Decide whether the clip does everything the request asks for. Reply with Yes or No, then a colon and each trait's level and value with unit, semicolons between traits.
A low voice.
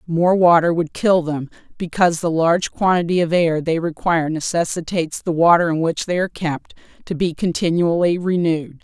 No: medium, 170 Hz